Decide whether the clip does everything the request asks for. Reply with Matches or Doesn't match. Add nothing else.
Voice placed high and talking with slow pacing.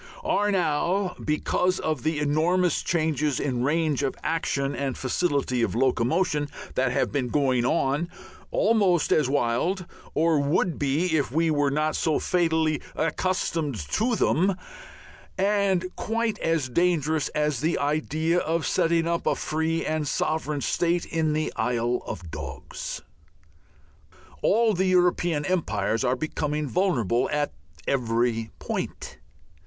Doesn't match